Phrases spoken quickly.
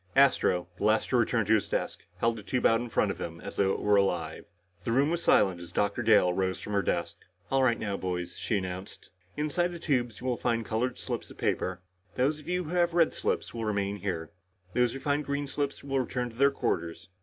Yes: fast, 235 wpm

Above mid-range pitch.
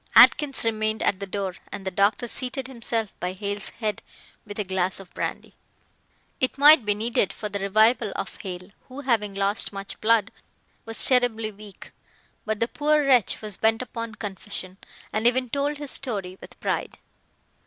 Yes: high, 215 Hz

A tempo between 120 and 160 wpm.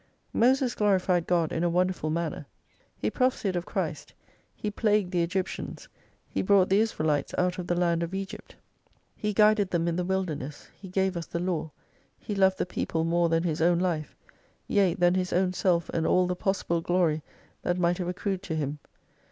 No: average, 190 wpm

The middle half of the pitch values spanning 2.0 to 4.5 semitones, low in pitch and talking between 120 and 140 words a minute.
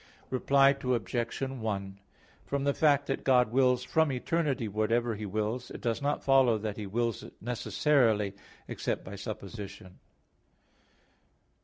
Yes: average, 4.2 semitones; low, 120 Hz; slow, 135 wpm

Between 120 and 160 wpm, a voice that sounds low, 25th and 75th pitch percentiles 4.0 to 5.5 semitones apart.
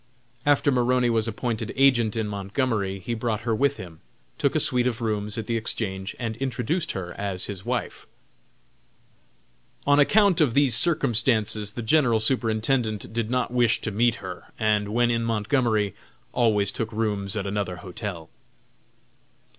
No: average, 155 wpm; low, 110 Hz; average, 3.0 semitones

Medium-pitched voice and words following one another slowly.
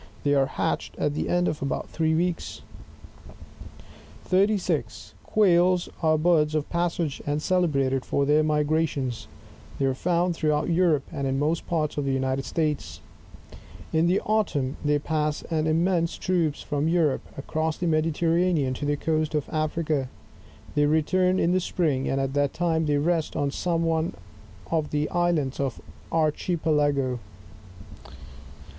No: medium, 155 Hz; average, 150 wpm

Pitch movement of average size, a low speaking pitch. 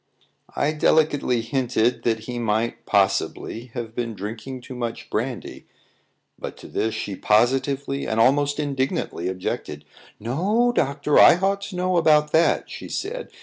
Yes: average, 4.8 semitones; low, 130 Hz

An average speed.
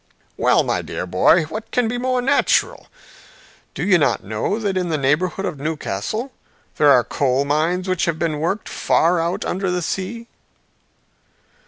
Yes: average, 165 wpm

